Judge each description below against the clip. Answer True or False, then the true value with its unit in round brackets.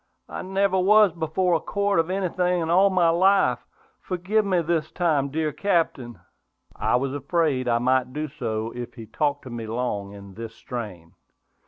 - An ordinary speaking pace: True (175 wpm)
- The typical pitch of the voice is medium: True (155 Hz)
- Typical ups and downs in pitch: False (6.8 semitones)